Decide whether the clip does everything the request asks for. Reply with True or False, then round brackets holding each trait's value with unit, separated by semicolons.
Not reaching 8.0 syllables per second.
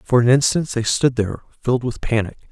True (6.1 syllables/s)